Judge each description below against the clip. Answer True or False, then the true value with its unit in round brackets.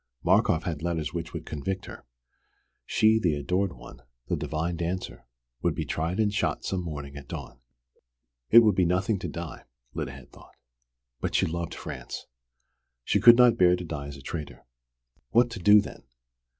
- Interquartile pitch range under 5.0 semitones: True (4.2 semitones)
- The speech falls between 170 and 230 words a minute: True (175 wpm)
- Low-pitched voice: True (85 Hz)